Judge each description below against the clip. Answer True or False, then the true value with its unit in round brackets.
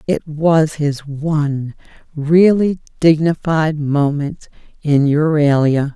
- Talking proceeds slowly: True (90 wpm)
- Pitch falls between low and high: True (150 Hz)